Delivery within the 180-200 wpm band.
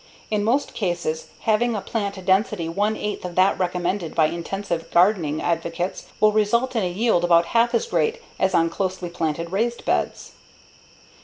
No: average, 165 wpm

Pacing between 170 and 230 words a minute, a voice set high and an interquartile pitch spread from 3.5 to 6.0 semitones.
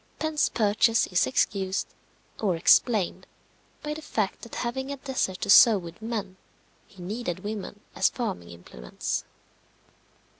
No: slow, 135 wpm; high, 210 Hz; average, 4.5 semitones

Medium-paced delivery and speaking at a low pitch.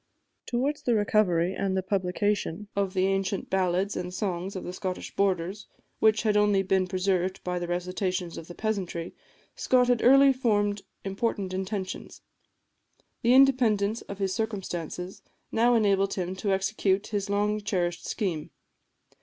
No: average, 145 wpm; high, 195 Hz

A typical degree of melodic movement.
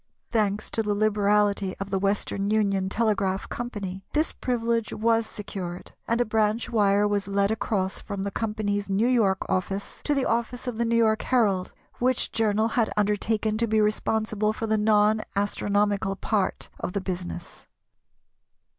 No: narrow, 2.1 semitones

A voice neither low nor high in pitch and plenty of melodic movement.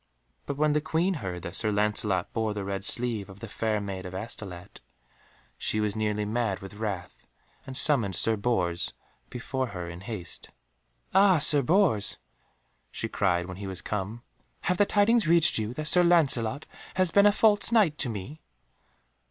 No: low, 110 Hz; wide, 7.6 semitones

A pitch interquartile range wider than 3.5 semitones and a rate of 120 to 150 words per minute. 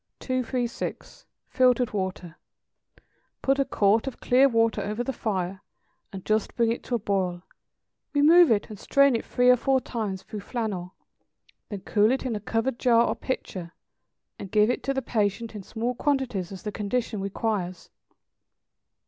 No: average, 3.9 semitones; average, 165 wpm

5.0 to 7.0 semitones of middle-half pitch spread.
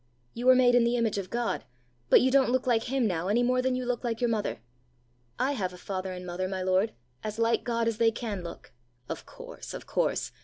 No: average, 4.2 semitones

